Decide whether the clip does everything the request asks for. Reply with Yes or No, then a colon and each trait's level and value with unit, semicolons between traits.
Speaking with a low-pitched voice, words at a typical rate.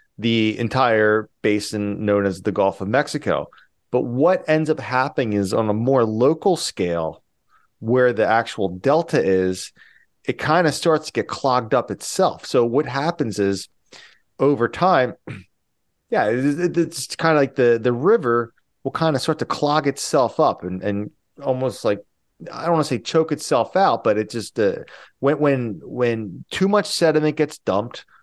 Yes: low, 120 Hz; average, 170 wpm